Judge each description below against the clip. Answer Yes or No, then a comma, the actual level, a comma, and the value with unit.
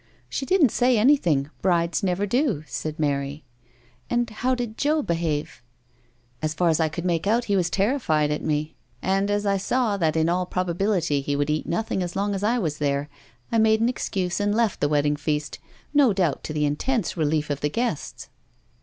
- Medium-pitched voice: Yes, medium, 175 Hz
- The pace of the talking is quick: Yes, fast, 210 wpm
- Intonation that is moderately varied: No, wide, 6.3 semitones